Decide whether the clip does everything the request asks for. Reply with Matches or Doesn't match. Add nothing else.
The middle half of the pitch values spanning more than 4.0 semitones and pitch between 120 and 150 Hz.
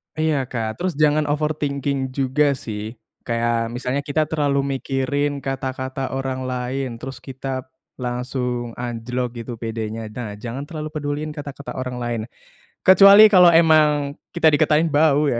Doesn't match